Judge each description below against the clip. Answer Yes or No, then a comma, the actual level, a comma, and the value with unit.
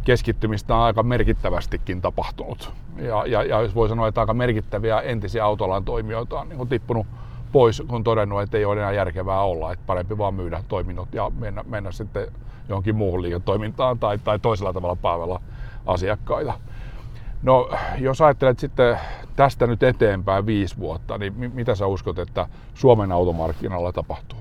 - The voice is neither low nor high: No, low, 110 Hz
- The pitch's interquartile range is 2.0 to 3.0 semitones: No, average, 3.4 semitones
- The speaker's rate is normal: No, fast, 160 wpm